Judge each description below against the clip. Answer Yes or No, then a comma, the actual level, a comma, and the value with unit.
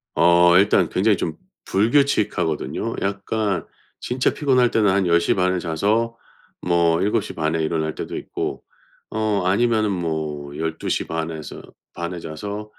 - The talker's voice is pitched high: No, very low, 90 Hz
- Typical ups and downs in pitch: Yes, average, 4.6 semitones